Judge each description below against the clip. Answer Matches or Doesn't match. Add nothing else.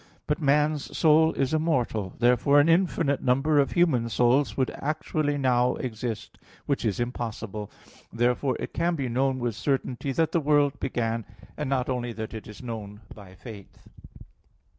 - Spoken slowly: Doesn't match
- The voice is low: Matches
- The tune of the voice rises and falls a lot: Doesn't match